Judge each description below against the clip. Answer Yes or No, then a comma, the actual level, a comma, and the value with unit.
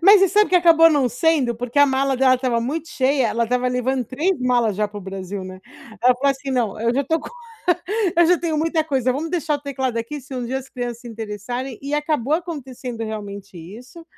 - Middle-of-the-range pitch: No, very high, 255 Hz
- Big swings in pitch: No, average, 4.2 semitones